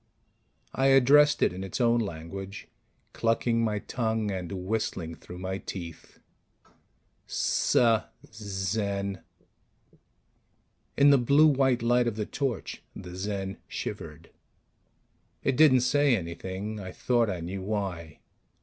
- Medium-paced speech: No, slow, 120 wpm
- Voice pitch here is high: No, low, 105 Hz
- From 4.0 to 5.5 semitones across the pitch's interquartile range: Yes, average, 4.4 semitones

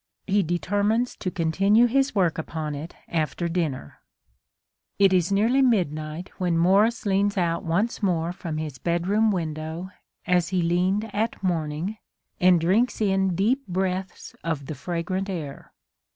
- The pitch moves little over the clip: No, average, 3.5 semitones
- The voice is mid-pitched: Yes, medium, 180 Hz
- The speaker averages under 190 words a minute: Yes, average, 140 wpm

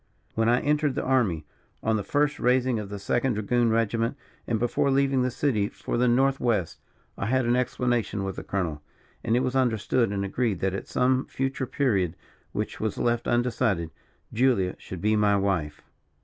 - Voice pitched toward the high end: No, low, 120 Hz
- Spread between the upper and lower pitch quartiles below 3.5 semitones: No, average, 4.1 semitones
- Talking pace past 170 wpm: Yes, average, 185 wpm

